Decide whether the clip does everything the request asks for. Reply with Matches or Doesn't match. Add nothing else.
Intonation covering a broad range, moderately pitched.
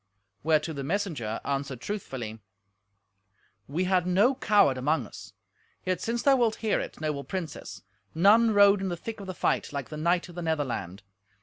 Matches